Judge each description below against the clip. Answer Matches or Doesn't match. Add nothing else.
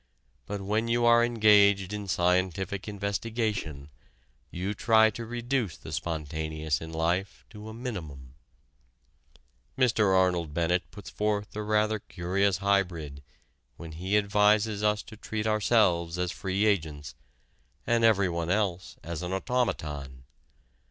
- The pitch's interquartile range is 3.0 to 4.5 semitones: Matches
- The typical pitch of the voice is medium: Doesn't match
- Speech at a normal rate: Doesn't match